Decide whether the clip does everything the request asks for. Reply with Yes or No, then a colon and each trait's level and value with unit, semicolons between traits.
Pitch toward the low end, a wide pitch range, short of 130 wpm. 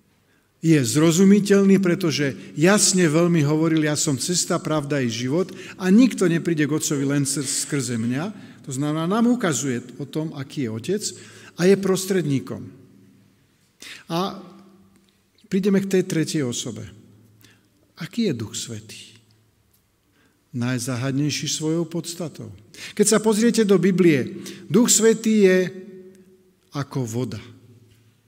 No: medium, 155 Hz; wide, 7.2 semitones; average, 115 wpm